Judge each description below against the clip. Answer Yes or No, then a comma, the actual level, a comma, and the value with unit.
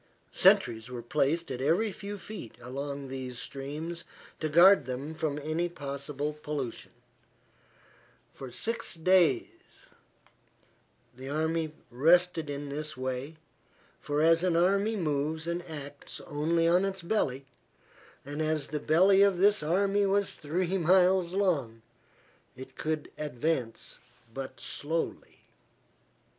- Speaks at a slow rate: Yes, slow, 120 wpm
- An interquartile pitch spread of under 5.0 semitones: Yes, average, 4.1 semitones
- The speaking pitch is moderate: Yes, medium, 155 Hz